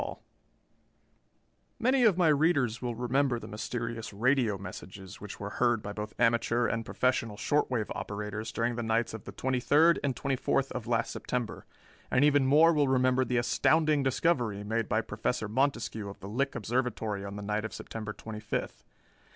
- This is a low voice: Yes, low, 120 Hz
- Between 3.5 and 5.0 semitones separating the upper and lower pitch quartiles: Yes, average, 3.8 semitones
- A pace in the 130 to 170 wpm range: No, average, 180 wpm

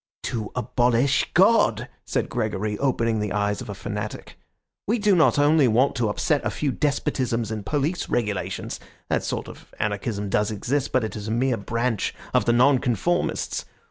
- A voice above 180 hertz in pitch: No, low, 120 Hz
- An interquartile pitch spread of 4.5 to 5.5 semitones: Yes, average, 4.8 semitones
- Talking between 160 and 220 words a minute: Yes, average, 170 wpm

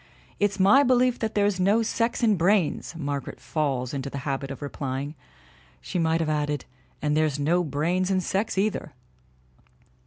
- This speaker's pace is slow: No, average, 160 wpm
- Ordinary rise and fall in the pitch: No, wide, 6.0 semitones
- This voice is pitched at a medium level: Yes, medium, 165 Hz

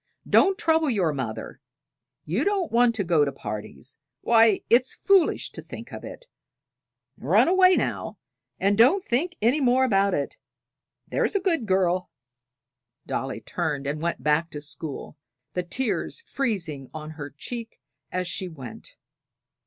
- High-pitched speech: Yes, high, 195 Hz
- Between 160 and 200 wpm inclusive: No, average, 145 wpm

